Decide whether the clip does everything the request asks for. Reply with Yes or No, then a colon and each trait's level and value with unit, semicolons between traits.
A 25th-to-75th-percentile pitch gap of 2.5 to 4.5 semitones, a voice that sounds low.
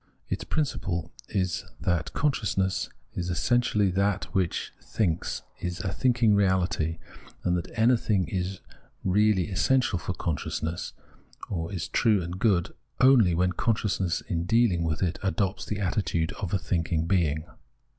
Yes: average, 3.4 semitones; very low, 95 Hz